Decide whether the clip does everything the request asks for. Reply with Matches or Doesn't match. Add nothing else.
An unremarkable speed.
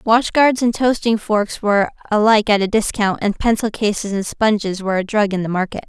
Doesn't match